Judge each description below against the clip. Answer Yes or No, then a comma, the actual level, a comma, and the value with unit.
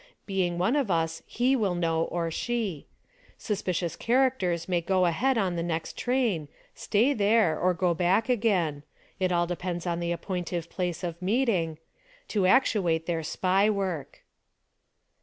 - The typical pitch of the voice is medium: Yes, medium, 180 Hz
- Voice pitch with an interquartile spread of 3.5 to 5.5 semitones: Yes, average, 4.1 semitones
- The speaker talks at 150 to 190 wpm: Yes, average, 160 wpm